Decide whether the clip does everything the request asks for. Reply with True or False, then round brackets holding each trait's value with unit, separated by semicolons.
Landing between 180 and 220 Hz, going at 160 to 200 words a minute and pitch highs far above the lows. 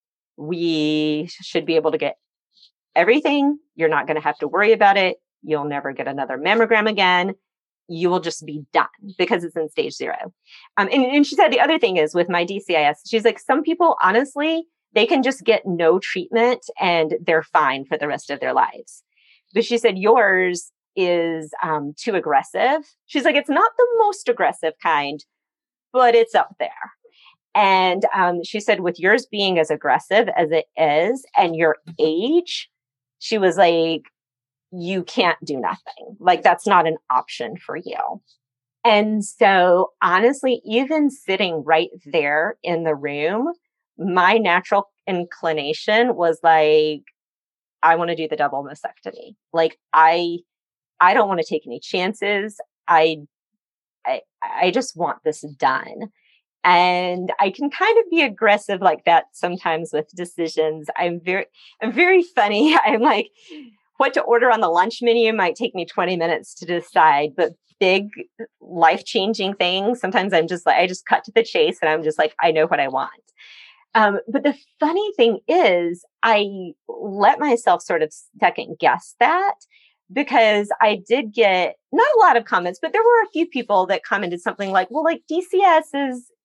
True (190 Hz; 170 wpm; 7.3 semitones)